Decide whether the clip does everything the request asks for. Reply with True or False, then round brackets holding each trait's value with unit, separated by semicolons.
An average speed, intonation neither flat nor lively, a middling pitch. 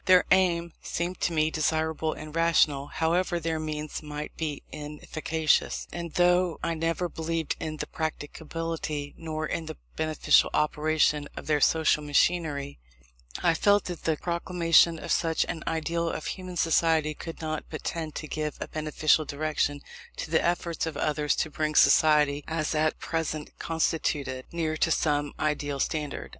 False (155 wpm; 1.6 semitones; 155 Hz)